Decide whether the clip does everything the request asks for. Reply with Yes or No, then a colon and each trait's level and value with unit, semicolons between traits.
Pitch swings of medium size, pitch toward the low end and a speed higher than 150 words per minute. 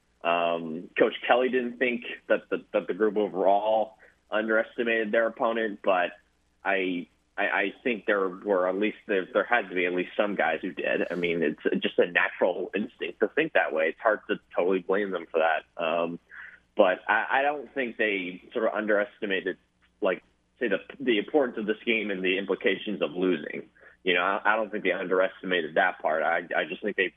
Yes: average, 4.4 semitones; low, 100 Hz; average, 200 wpm